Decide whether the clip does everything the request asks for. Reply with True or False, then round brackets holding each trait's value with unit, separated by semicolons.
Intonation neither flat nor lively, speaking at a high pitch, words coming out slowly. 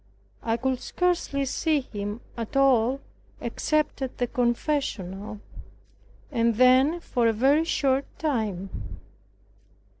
True (4.0 semitones; 255 Hz; 110 wpm)